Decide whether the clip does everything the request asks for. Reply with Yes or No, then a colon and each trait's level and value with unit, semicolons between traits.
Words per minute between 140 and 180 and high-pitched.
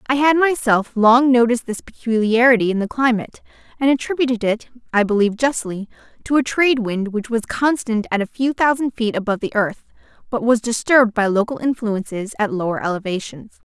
Yes: average, 175 wpm; high, 230 Hz